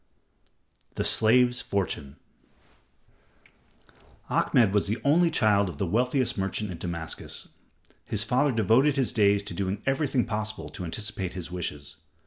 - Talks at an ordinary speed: No, slow, 130 wpm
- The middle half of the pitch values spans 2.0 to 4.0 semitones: No, average, 4.8 semitones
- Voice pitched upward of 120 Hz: No, low, 105 Hz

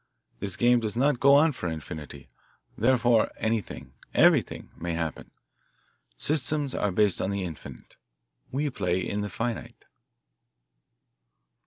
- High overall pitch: No, low, 110 Hz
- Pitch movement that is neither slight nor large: No, wide, 6.2 semitones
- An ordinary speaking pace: No, slow, 125 wpm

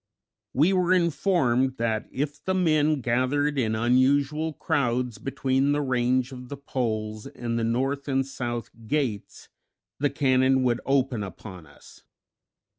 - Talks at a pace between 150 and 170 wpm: No, slow, 135 wpm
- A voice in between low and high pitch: No, low, 130 Hz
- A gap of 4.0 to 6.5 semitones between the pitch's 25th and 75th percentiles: No, average, 3.3 semitones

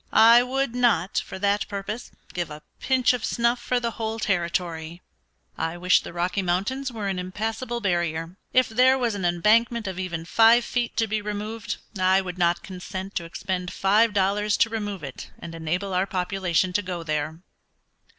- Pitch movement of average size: Yes, average, 4.3 semitones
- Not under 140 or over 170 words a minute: No, average, 180 wpm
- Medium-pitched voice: No, high, 195 Hz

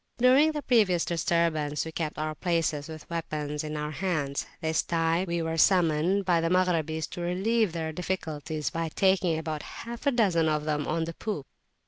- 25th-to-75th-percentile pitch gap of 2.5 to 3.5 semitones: Yes, average, 2.9 semitones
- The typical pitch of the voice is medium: Yes, medium, 165 Hz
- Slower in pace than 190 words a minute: Yes, average, 180 wpm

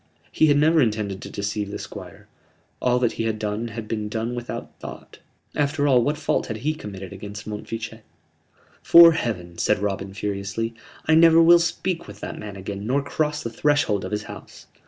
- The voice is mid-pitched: No, low, 115 Hz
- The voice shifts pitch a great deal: Yes, wide, 6.0 semitones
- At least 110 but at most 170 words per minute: No, average, 190 wpm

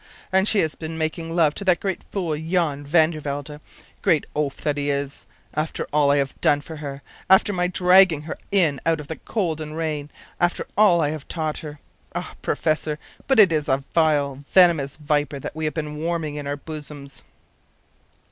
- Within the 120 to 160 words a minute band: No, average, 195 wpm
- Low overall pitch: No, medium, 155 Hz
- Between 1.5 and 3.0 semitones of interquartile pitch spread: Yes, narrow, 2.6 semitones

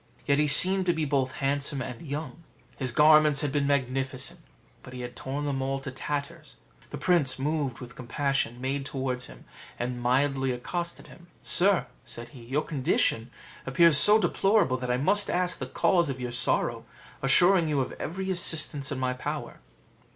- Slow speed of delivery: No, average, 175 wpm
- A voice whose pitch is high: No, medium, 140 Hz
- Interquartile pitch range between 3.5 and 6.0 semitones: Yes, average, 3.8 semitones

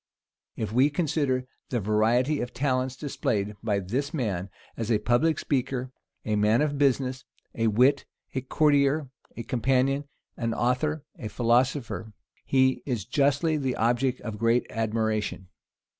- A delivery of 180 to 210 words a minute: No, average, 140 wpm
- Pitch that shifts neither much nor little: Yes, average, 3.6 semitones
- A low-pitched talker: Yes, low, 125 Hz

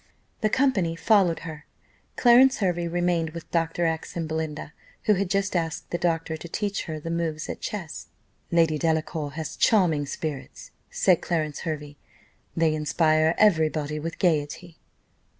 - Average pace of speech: Yes, average, 150 wpm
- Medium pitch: Yes, medium, 165 Hz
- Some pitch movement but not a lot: No, narrow, 2.1 semitones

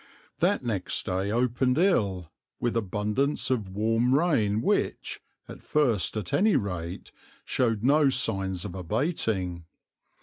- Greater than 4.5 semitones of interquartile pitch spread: Yes, average, 5.3 semitones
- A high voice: No, low, 110 Hz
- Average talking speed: No, slow, 125 wpm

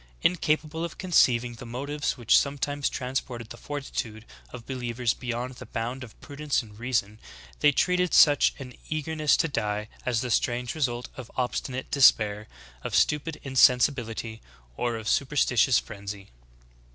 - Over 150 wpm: No, average, 145 wpm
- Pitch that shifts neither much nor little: Yes, average, 3.8 semitones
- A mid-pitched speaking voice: No, low, 125 Hz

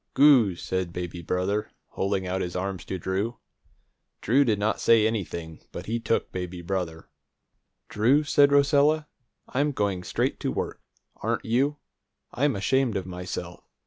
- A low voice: Yes, low, 105 Hz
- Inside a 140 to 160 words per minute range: Yes, average, 145 wpm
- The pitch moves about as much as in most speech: No, wide, 6.3 semitones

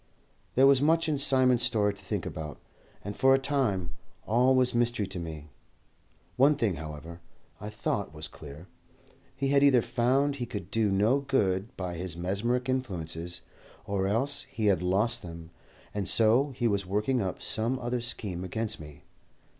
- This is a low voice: Yes, low, 105 Hz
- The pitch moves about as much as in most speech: No, wide, 5.9 semitones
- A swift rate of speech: No, average, 170 wpm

